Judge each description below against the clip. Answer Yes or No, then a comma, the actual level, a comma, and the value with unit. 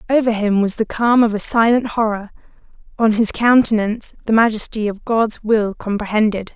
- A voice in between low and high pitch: No, high, 220 Hz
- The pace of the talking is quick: No, average, 165 wpm